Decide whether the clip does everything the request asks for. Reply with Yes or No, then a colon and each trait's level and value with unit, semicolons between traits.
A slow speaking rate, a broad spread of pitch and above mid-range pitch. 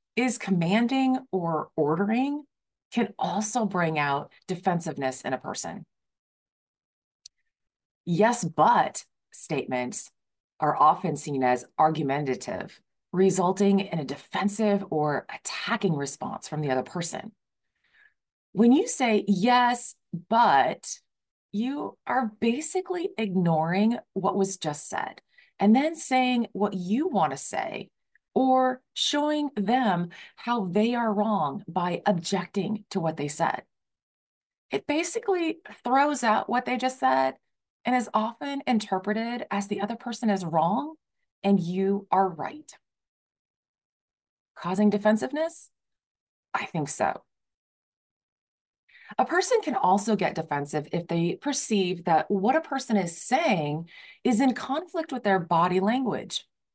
Yes: slow, 120 wpm; wide, 6.3 semitones; high, 205 Hz